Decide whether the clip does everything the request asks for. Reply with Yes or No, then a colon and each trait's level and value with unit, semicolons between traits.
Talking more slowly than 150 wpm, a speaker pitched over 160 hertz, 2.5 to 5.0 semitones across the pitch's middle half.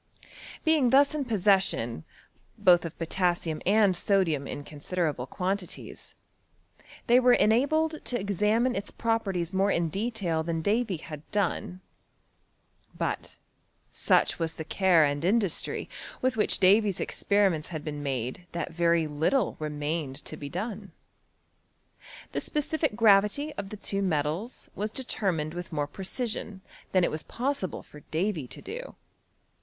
No: average, 140 wpm; high, 190 Hz; wide, 5.4 semitones